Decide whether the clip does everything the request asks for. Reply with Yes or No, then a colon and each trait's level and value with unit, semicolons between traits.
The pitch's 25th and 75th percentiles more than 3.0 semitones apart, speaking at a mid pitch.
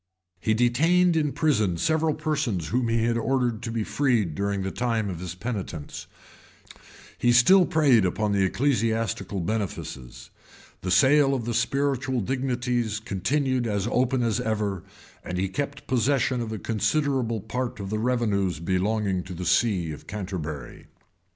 No: average, 4.9 semitones; low, 115 Hz